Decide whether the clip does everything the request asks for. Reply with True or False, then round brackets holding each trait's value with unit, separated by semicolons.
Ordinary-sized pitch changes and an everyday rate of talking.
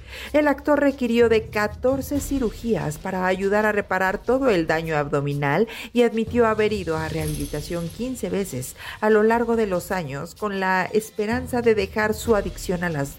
True (4.8 semitones; 170 wpm)